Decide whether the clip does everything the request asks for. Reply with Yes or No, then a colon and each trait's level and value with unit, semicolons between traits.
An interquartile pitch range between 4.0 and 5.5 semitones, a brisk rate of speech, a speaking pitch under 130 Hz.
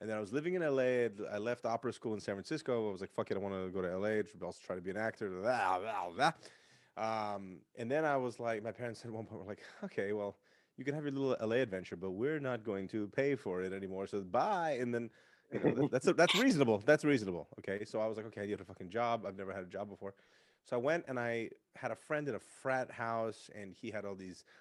Yes: average, 4.3 semitones; fast, 265 wpm; low, 110 Hz